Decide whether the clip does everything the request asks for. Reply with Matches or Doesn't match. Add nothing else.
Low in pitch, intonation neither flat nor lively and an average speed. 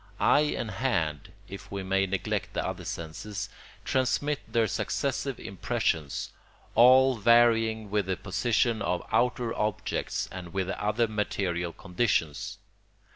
Doesn't match